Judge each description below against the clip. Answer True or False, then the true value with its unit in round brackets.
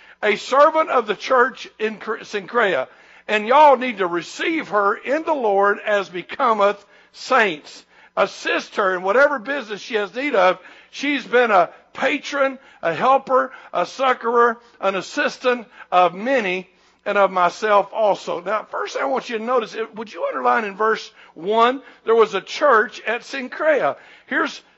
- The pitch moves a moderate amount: True (4.6 semitones)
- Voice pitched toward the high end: True (230 Hz)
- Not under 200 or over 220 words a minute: False (155 wpm)